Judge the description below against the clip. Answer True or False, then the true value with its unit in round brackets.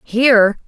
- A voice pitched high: True (225 Hz)